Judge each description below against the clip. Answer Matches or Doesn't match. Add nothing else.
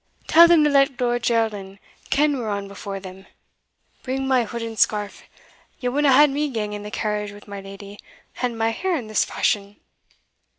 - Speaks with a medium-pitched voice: Doesn't match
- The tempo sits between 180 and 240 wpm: Matches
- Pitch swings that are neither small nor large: Matches